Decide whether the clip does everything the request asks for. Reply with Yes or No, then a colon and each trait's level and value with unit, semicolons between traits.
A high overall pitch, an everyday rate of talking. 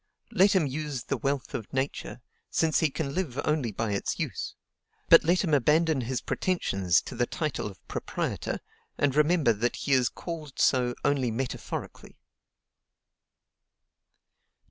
No: medium, 140 Hz; average, 145 wpm